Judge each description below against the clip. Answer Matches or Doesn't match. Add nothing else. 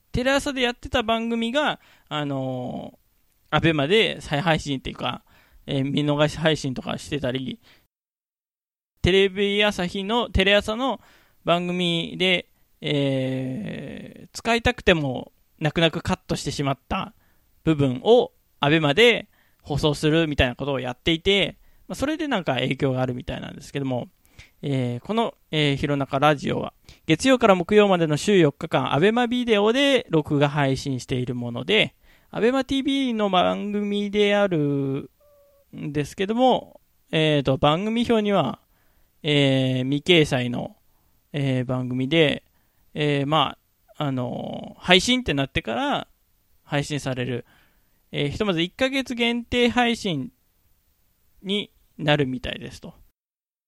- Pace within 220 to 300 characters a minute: Matches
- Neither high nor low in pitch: Matches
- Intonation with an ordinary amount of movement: Doesn't match